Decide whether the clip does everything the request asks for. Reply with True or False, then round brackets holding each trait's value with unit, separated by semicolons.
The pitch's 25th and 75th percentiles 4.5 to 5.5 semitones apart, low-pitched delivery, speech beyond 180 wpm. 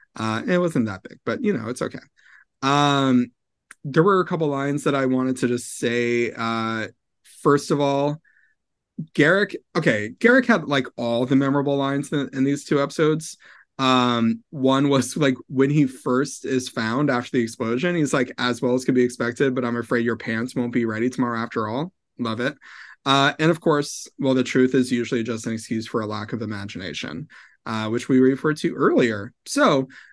False (3.2 semitones; 130 Hz; 195 wpm)